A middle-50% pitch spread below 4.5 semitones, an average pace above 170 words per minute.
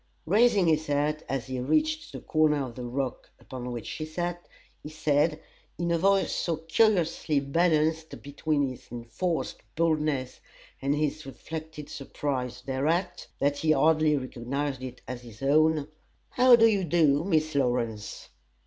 No: average, 3.3 semitones; average, 150 wpm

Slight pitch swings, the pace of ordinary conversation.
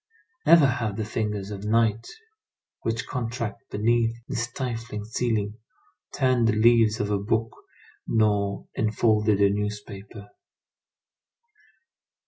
No: narrow, 2.0 semitones; slow, 110 wpm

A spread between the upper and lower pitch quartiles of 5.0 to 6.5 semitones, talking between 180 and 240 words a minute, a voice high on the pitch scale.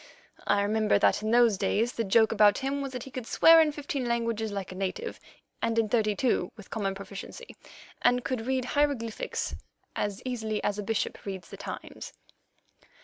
No: average, 3.5 semitones; average, 185 wpm; high, 225 Hz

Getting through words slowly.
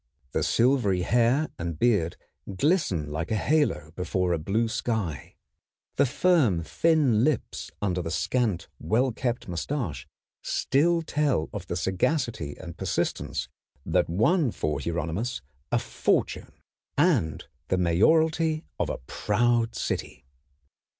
Yes: slow, 125 wpm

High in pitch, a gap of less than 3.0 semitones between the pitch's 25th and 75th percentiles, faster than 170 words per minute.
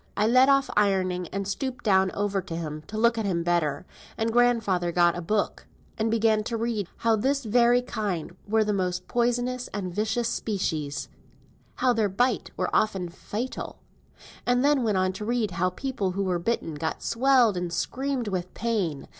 No: high, 210 Hz; average, 4.5 semitones; average, 180 wpm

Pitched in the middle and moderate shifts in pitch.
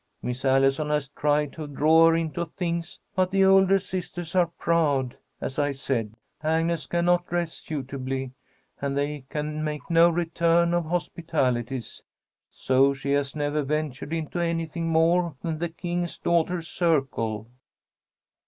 Yes: medium, 160 Hz; average, 3.5 semitones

